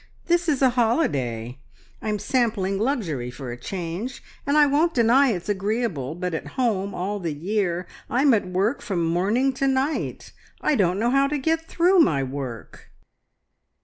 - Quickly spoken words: No, average, 165 wpm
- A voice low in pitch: No, high, 210 Hz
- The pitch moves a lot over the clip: Yes, wide, 7.6 semitones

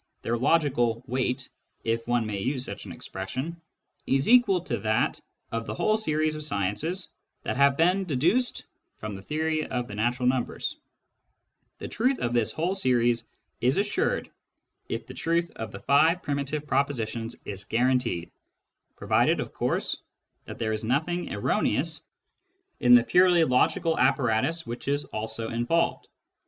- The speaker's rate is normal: Yes, average, 150 wpm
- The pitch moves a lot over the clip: Yes, wide, 6.0 semitones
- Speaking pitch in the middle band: No, low, 130 Hz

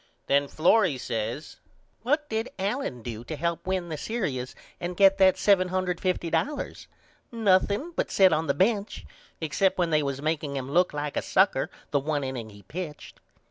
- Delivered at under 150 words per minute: No, average, 165 wpm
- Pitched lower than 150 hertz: No, medium, 170 Hz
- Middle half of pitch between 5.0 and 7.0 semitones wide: Yes, wide, 5.4 semitones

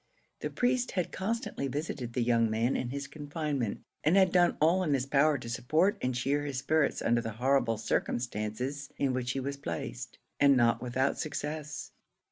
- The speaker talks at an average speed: Yes, average, 180 wpm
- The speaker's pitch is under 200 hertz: Yes, medium, 140 Hz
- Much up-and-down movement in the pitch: No, average, 4.0 semitones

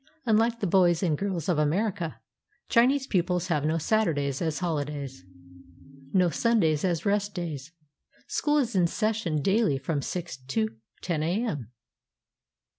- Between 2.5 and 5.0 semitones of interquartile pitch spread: No, wide, 5.6 semitones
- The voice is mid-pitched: Yes, medium, 175 Hz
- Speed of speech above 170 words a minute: No, slow, 135 wpm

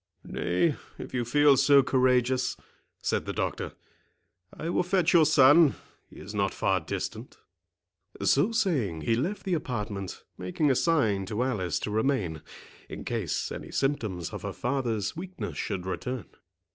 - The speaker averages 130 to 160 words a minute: Yes, average, 145 wpm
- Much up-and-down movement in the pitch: Yes, wide, 6.4 semitones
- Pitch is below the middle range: Yes, low, 125 Hz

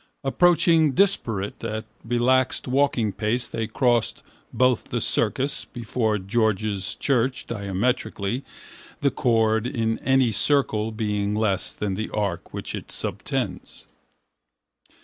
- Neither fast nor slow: No, slow, 110 wpm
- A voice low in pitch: Yes, low, 115 Hz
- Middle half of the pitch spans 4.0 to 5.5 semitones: No, average, 3.4 semitones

